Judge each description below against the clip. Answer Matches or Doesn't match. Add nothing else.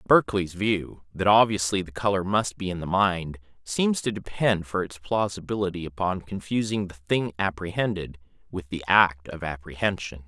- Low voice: Matches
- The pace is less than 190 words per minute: Matches